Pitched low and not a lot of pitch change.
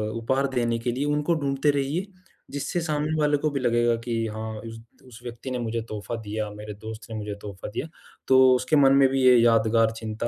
No: low, 120 Hz; average, 3.8 semitones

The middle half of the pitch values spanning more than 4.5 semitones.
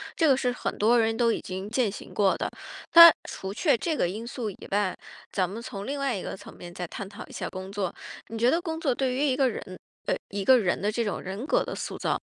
Yes: average, 4.9 semitones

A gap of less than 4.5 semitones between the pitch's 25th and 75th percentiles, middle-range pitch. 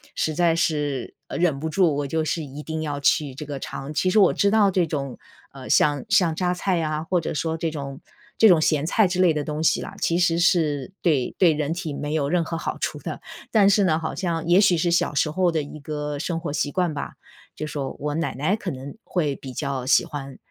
Yes: average, 3.3 semitones; medium, 160 Hz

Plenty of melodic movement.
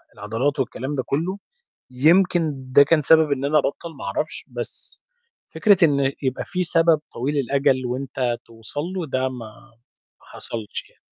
No: average, 3.9 semitones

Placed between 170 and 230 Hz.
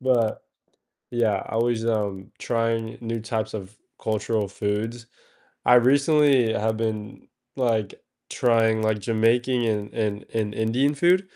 No: low, 115 Hz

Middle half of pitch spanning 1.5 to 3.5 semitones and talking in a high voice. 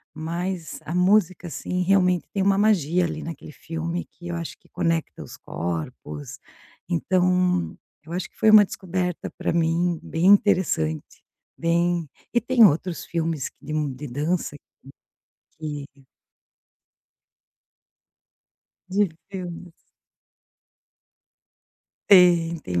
No: narrow, 2.4 semitones; medium, 170 Hz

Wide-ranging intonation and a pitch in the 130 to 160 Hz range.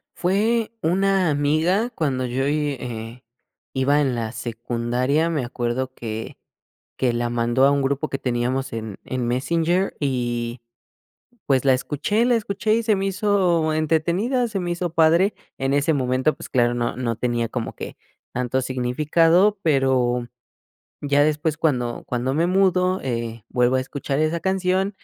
Yes: wide, 5.9 semitones; medium, 140 Hz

